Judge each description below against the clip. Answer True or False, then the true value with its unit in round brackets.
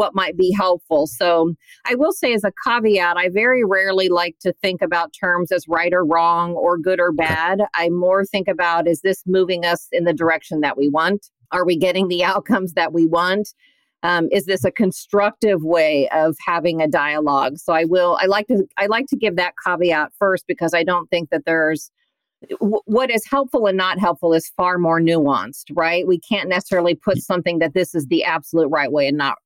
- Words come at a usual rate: False (210 wpm)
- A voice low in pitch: False (175 Hz)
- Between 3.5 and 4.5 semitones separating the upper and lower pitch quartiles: False (2.7 semitones)